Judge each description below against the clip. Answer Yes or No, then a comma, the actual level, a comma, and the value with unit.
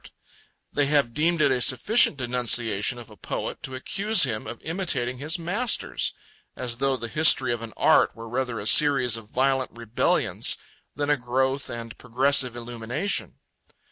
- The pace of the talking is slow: No, average, 165 wpm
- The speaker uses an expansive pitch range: No, average, 3.5 semitones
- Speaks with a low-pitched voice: Yes, low, 130 Hz